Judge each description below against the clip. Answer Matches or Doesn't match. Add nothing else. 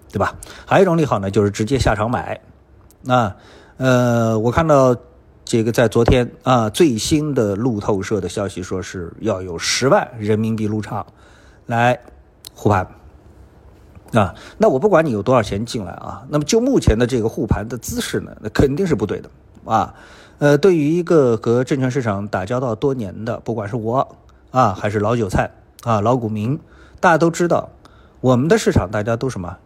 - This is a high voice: Doesn't match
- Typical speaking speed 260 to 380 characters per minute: Matches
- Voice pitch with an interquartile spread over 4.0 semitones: Doesn't match